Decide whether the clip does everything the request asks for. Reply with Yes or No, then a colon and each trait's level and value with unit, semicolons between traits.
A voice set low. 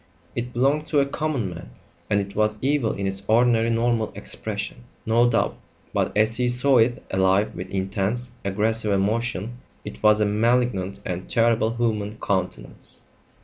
Yes: low, 110 Hz